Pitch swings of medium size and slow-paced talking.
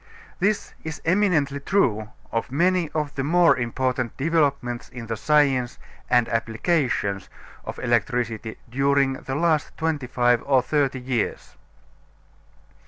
Yes: average, 4.1 semitones; slow, 120 wpm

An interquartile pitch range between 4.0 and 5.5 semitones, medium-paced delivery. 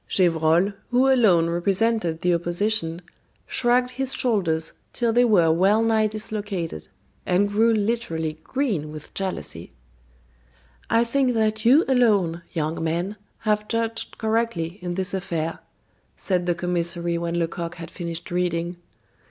No: average, 5.0 semitones; slow, 130 wpm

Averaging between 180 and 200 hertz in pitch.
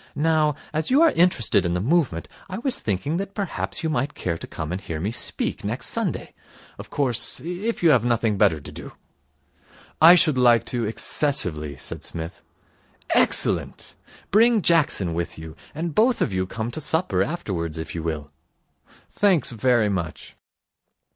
No: low, 120 Hz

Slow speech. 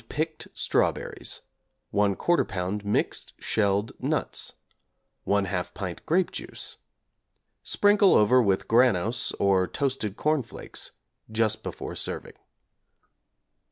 Yes: slow, 95 wpm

